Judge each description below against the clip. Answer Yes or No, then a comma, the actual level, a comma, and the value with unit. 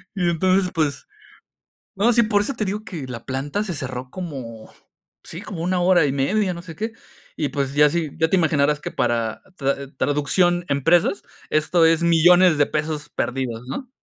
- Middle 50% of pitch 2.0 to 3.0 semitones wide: No, average, 4.6 semitones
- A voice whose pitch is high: No, medium, 160 Hz